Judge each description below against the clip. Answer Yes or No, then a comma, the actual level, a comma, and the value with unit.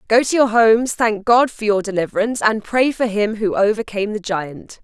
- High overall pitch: Yes, high, 215 Hz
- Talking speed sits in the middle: No, fast, 210 wpm